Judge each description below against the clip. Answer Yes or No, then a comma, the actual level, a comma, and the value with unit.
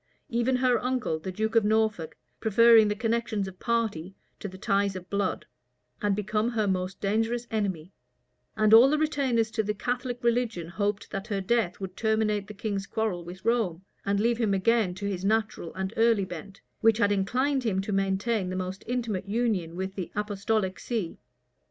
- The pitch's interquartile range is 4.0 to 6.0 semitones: No, average, 3.2 semitones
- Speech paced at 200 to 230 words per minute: No, average, 180 wpm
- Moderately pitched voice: No, high, 210 Hz